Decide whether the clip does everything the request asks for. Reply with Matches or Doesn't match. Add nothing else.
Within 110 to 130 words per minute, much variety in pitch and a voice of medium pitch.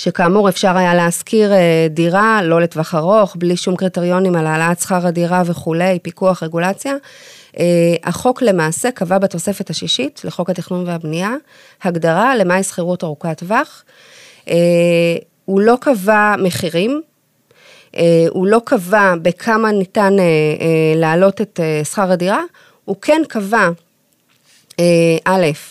Doesn't match